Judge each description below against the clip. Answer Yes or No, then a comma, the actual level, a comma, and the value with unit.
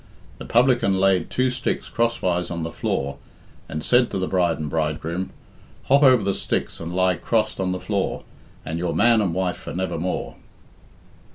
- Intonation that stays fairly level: No, average, 4.6 semitones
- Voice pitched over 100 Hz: No, very low, 95 Hz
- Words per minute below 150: No, average, 175 wpm